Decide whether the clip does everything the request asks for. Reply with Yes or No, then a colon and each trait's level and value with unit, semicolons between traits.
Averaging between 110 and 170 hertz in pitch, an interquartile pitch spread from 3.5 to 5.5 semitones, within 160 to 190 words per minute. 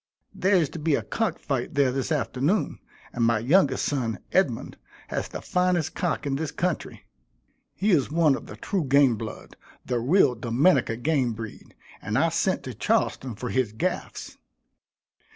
Yes: medium, 140 Hz; average, 5.2 semitones; average, 170 wpm